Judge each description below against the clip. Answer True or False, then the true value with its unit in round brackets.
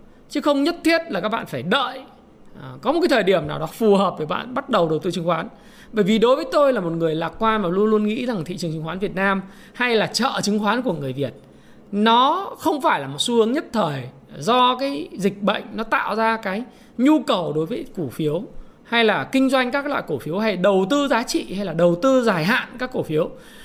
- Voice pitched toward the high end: True (220 Hz)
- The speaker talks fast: True (255 wpm)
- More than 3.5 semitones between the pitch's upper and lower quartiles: True (5.6 semitones)